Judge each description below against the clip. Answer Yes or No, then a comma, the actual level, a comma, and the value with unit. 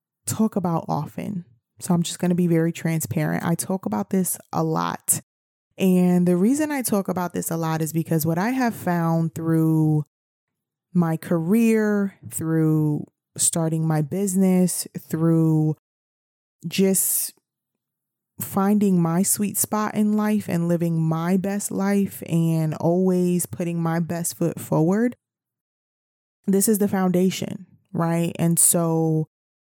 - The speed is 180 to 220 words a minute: No, slow, 135 wpm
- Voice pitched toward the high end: No, medium, 175 Hz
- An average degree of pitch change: Yes, average, 3.1 semitones